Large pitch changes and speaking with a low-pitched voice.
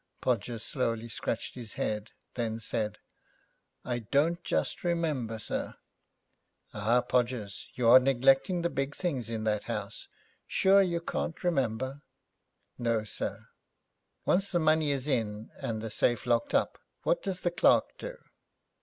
Yes: wide, 5.8 semitones; low, 125 Hz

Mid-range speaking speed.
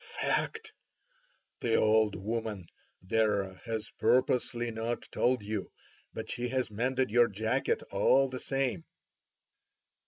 No: slow, 115 wpm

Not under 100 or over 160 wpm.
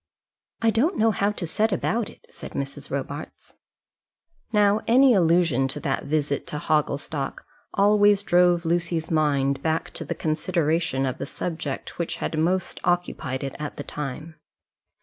Yes: average, 150 wpm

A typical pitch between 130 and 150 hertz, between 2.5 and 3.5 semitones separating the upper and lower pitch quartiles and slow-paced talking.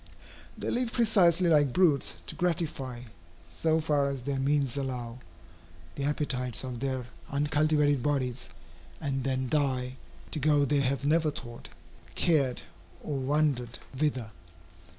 Yes: medium, 140 Hz; average, 2.9 semitones; slow, 130 wpm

